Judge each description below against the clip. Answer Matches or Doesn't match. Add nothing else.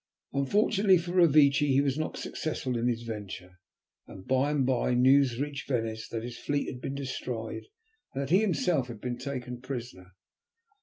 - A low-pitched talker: Matches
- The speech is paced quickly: Doesn't match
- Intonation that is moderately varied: Matches